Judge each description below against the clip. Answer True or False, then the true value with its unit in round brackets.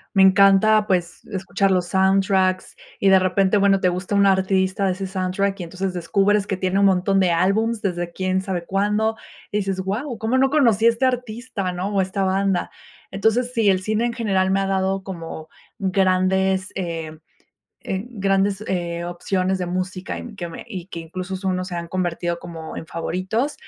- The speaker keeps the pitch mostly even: True (1.6 semitones)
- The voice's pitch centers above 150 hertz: True (190 Hz)